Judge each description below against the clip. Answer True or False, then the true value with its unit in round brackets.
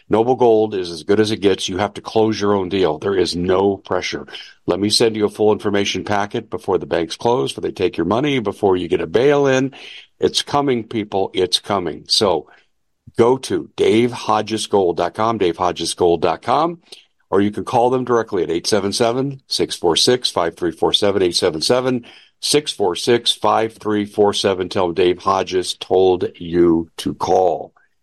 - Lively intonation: False (4.2 semitones)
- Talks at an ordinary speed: True (150 wpm)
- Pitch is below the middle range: True (110 Hz)